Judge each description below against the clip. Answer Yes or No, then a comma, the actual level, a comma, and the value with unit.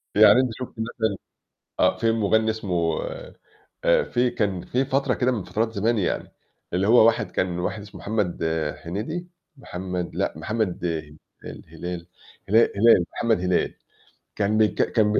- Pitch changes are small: No, average, 4.2 semitones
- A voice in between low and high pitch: No, low, 105 Hz